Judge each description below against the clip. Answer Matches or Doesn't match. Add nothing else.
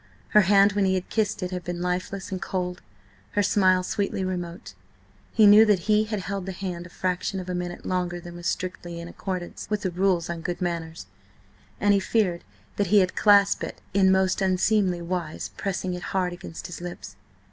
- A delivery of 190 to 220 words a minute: Matches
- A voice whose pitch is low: Doesn't match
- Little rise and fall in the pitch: Matches